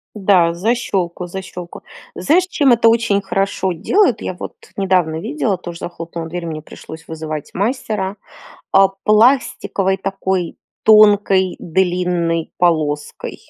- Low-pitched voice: No, high, 190 Hz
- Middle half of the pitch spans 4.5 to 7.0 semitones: No, average, 3.7 semitones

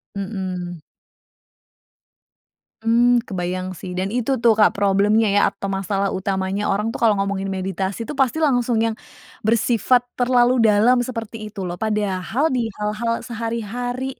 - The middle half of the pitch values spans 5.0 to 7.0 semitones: No, average, 3.2 semitones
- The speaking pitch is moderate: No, high, 210 Hz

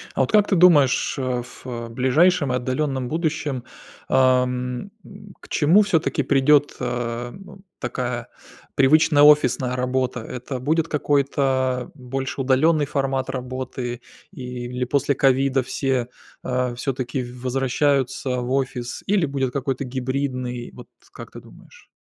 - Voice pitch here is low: Yes, low, 130 Hz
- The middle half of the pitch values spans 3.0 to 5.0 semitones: No, narrow, 2.4 semitones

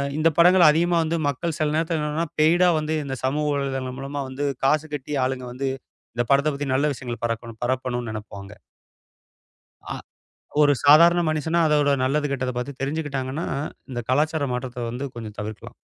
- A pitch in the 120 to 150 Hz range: Yes, medium, 140 Hz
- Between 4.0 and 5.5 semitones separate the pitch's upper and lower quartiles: No, average, 3.3 semitones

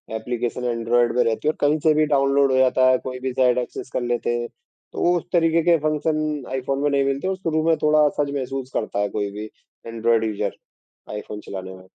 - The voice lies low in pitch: Yes, low, 130 Hz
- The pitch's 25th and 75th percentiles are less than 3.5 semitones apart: No, average, 4.3 semitones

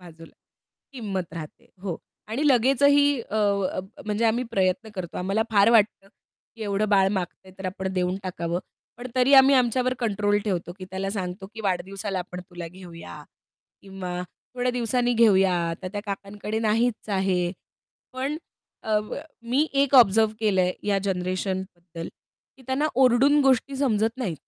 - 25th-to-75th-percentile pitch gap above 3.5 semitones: Yes, average, 4.4 semitones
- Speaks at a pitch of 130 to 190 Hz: No, high, 205 Hz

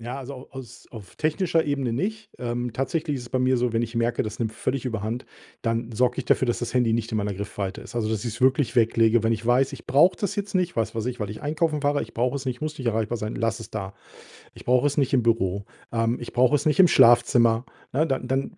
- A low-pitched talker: Yes, low, 120 Hz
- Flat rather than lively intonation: No, average, 3.1 semitones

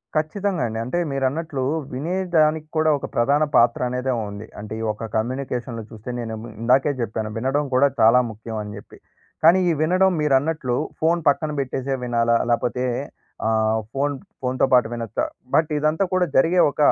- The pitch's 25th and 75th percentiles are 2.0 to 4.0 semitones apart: No, average, 4.9 semitones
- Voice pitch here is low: Yes, low, 130 Hz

